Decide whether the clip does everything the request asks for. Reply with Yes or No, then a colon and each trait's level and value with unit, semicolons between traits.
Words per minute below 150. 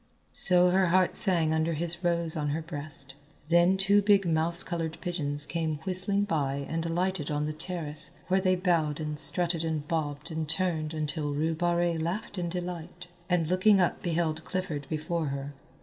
No: average, 175 wpm